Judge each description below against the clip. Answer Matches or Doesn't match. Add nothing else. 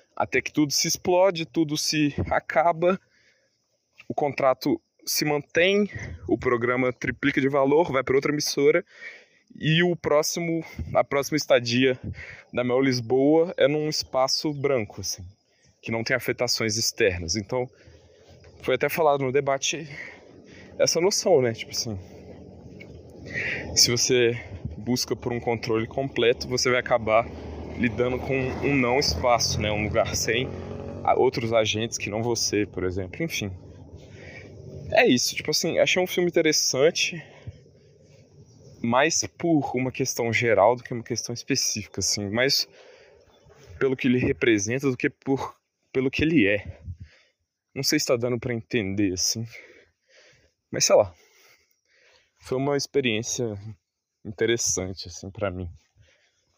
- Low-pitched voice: Matches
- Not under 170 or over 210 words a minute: Doesn't match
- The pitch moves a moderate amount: Matches